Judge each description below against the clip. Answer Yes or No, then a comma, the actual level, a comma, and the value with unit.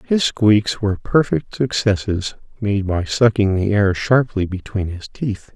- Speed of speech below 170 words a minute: Yes, average, 140 wpm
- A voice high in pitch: No, low, 105 Hz